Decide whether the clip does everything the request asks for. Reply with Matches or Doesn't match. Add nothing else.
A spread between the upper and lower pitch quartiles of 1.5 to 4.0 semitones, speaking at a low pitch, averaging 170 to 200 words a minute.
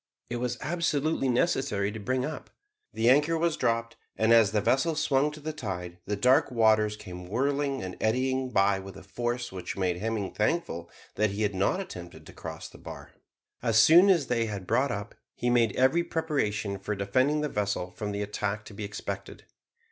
Doesn't match